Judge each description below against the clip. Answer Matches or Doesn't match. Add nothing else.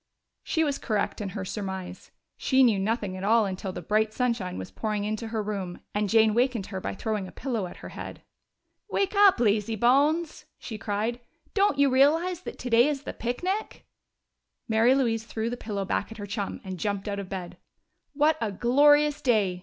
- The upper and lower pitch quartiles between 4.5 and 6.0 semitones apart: Matches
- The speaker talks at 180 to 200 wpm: Matches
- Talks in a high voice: Matches